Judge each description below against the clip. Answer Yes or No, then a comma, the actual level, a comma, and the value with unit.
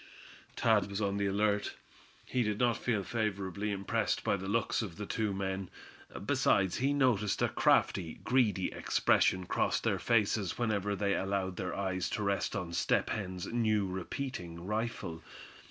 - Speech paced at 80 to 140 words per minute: No, average, 155 wpm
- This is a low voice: Yes, low, 100 Hz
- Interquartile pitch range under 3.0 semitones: Yes, narrow, 2.4 semitones